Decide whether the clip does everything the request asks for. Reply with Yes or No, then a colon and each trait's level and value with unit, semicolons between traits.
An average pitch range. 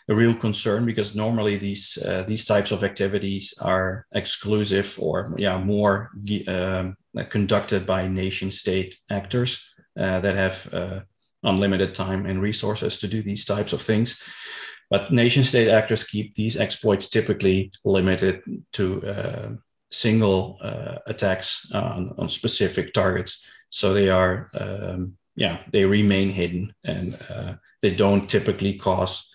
No: narrow, 2.3 semitones